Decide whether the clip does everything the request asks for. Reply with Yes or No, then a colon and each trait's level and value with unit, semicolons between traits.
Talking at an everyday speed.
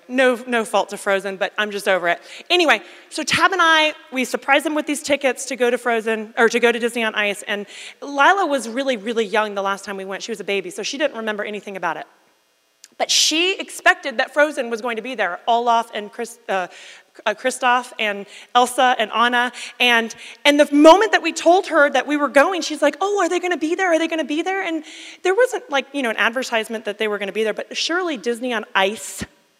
No: fast, 245 wpm